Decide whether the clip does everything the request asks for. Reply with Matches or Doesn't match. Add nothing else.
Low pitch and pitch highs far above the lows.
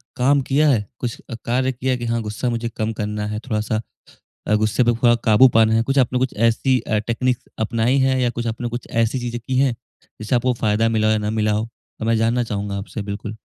Doesn't match